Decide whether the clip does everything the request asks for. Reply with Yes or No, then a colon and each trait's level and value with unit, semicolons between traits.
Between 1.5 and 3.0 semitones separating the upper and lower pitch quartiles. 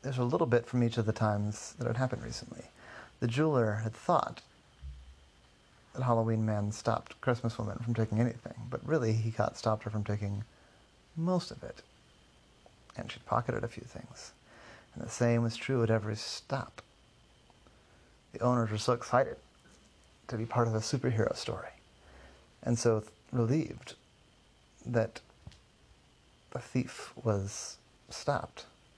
Yes: narrow, 2.6 semitones